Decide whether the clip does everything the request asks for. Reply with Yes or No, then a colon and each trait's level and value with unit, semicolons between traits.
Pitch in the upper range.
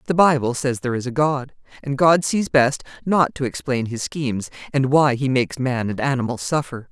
No: low, 135 Hz